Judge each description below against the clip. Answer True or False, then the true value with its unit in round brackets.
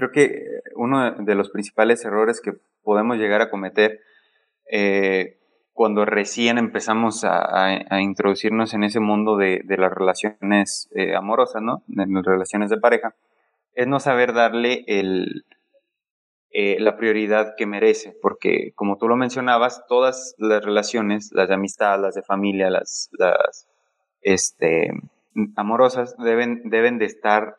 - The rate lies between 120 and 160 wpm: True (145 wpm)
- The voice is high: False (110 Hz)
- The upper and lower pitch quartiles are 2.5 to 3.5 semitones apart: True (3.0 semitones)